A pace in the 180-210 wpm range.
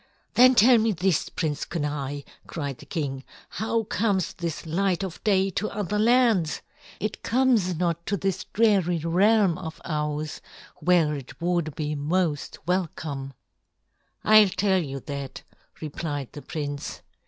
No: average, 140 wpm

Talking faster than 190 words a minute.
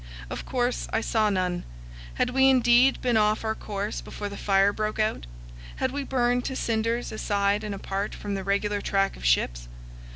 No: average, 185 wpm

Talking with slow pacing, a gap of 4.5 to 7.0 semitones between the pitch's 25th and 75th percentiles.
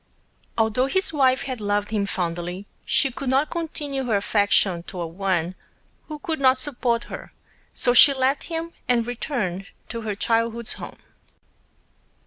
No: average, 145 wpm; average, 5.1 semitones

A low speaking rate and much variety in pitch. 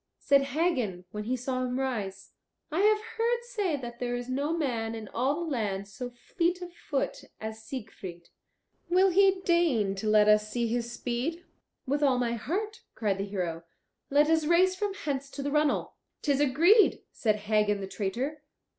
No: average, 180 wpm; wide, 7.2 semitones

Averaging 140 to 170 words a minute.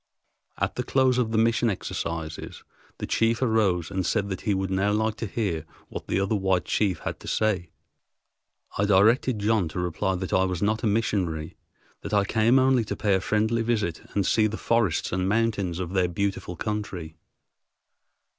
No: average, 185 wpm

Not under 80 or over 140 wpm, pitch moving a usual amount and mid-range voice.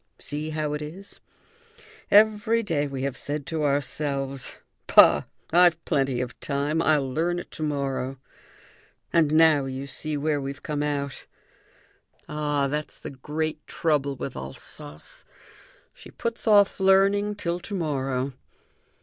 Yes: slow, 135 wpm; average, 3.1 semitones; medium, 150 Hz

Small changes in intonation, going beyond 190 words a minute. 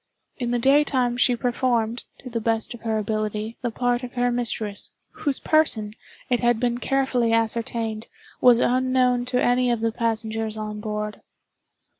No: narrow, 2.0 semitones; average, 155 wpm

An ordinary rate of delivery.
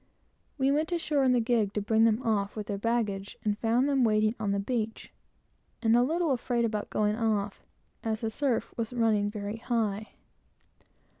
Yes: average, 180 wpm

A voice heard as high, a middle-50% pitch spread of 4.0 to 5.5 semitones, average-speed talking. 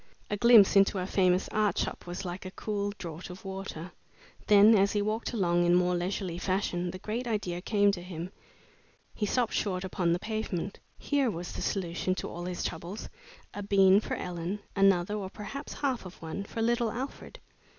No: high, 195 Hz; average, 2.8 semitones; average, 190 wpm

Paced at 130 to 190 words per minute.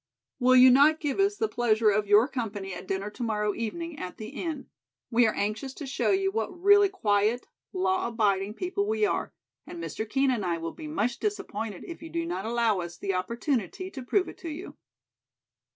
No: fast, 205 wpm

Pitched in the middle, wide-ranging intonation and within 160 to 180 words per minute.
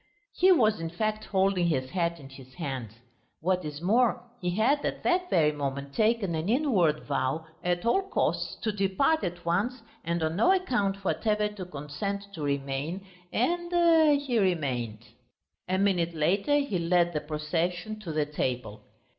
Yes: medium, 180 Hz; wide, 6.1 semitones; average, 165 wpm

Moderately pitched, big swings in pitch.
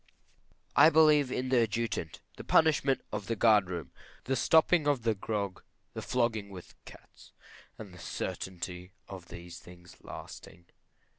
No: low, 110 Hz; wide, 6.5 semitones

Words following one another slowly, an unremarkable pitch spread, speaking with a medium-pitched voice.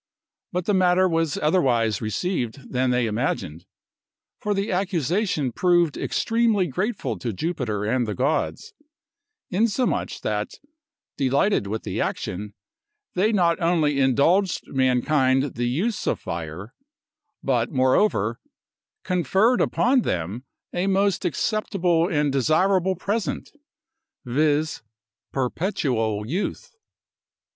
No: slow, 105 wpm; wide, 7.2 semitones; medium, 155 Hz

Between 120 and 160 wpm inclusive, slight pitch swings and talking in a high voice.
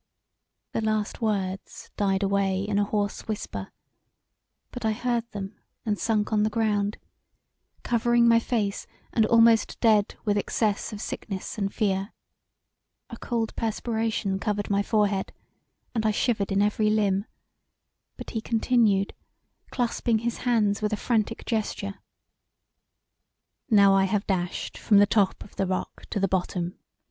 Yes: average, 145 wpm; narrow, 2.1 semitones; high, 210 Hz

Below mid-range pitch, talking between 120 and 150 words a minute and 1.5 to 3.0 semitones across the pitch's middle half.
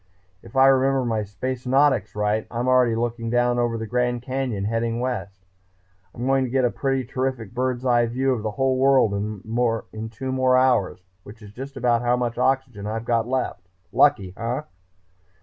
No: low, 120 Hz; average, 180 wpm; narrow, 2.5 semitones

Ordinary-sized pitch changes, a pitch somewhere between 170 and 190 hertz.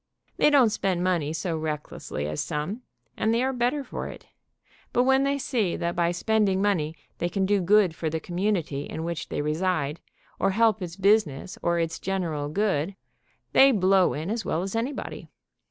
Yes: average, 4.9 semitones; medium, 185 Hz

